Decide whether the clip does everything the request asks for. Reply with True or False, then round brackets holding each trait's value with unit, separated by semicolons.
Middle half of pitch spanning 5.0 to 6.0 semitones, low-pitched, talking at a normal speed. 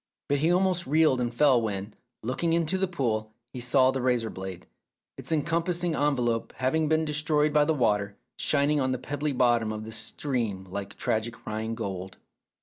True (5.4 semitones; 130 Hz; 180 wpm)